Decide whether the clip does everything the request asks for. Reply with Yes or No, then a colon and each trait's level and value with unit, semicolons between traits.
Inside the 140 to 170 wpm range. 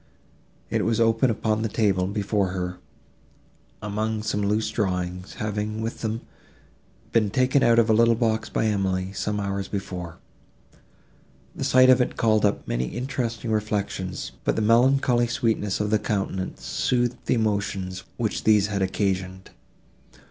Yes: average, 150 wpm